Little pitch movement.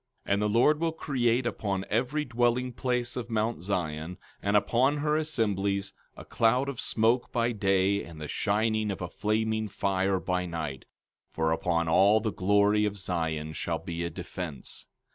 No: average, 4.6 semitones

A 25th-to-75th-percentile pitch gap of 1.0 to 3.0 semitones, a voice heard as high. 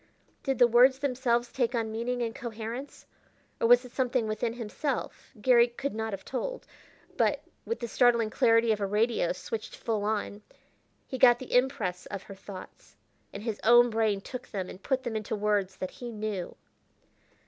Yes: narrow, 2.6 semitones; high, 230 Hz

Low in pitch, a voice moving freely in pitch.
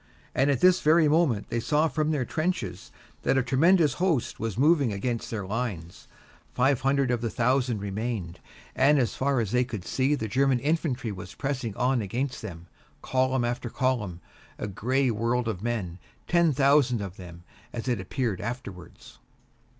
No: low, 125 Hz; average, 4.2 semitones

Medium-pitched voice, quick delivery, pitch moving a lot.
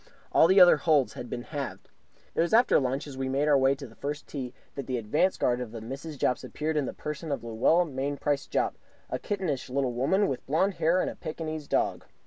No: medium, 145 Hz; fast, 230 wpm; average, 3.3 semitones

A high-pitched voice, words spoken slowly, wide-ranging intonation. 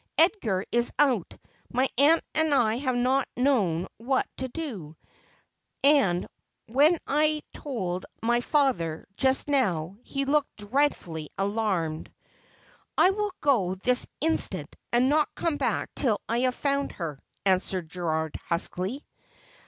Yes: high, 245 Hz; slow, 130 wpm; wide, 7.3 semitones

